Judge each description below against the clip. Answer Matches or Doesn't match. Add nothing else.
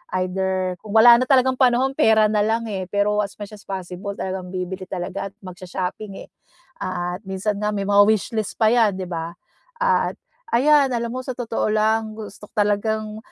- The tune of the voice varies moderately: Matches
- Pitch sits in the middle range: Doesn't match